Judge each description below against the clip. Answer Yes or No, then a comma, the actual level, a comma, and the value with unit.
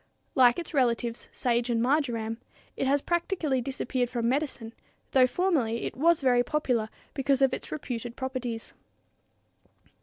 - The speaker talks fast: No, average, 140 wpm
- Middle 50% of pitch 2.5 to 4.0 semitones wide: Yes, average, 3.0 semitones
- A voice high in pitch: Yes, very high, 255 Hz